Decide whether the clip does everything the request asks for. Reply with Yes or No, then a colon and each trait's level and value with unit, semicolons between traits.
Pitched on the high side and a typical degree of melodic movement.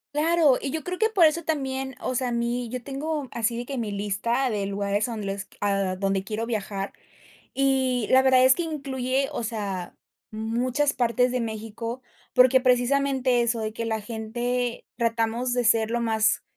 Yes: high, 240 Hz; average, 3.1 semitones